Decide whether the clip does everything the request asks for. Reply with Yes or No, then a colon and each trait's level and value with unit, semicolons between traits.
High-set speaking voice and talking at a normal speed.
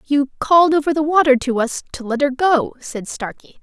No: very high, 280 Hz; fast, 215 wpm